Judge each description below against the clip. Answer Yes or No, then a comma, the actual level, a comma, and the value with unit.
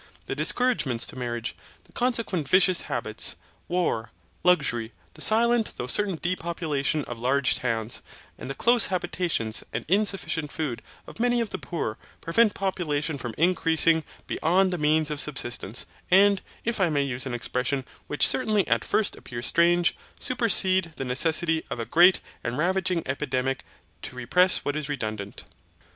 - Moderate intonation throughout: No, wide, 6.6 semitones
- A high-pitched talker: No, medium, 160 Hz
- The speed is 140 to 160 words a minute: Yes, average, 150 wpm